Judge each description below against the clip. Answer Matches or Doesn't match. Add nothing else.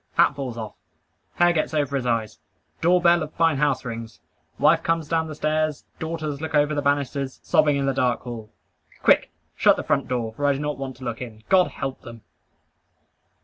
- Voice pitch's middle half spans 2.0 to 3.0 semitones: Doesn't match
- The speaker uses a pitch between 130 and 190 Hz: Matches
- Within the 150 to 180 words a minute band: Doesn't match